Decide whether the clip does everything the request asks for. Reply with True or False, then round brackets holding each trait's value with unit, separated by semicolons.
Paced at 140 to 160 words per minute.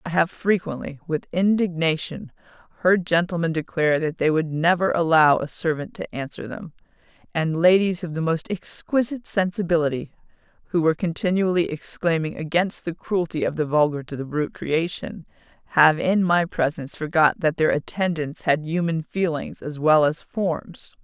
True (155 wpm)